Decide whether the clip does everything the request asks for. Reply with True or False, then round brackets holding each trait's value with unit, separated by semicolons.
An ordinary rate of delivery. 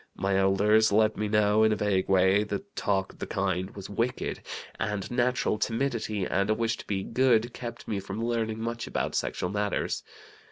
True (190 wpm)